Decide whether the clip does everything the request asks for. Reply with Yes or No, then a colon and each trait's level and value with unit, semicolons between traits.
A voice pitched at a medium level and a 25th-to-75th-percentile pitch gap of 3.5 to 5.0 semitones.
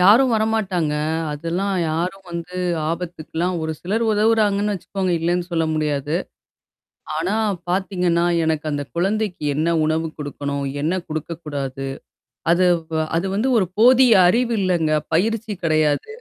Yes: medium, 175 Hz; average, 4.2 semitones